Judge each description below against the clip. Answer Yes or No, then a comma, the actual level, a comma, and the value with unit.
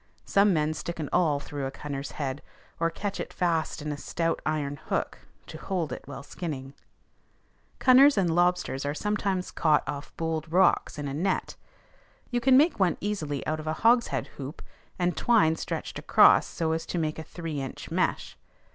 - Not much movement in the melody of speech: No, average, 4.0 semitones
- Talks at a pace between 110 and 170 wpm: No, average, 180 wpm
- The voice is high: No, medium, 160 Hz